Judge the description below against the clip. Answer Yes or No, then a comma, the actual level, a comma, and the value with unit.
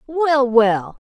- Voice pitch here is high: Yes, very high, 255 Hz